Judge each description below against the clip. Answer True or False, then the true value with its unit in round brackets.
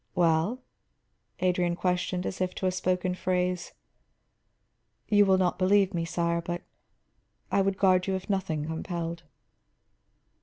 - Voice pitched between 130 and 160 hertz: False (180 Hz)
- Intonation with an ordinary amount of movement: False (1.6 semitones)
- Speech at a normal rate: False (130 wpm)